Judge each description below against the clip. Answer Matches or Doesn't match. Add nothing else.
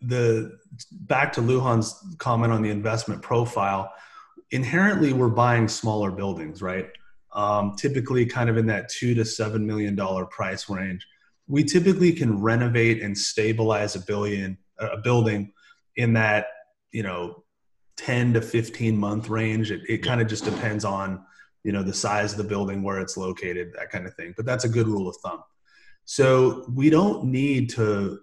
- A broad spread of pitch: Doesn't match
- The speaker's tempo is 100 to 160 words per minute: Doesn't match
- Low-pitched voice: Matches